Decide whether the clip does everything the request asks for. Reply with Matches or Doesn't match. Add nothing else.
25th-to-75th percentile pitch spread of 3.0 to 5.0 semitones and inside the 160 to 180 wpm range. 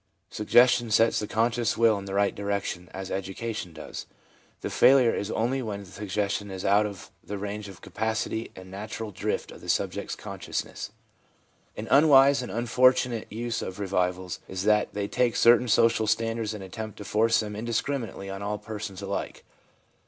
Doesn't match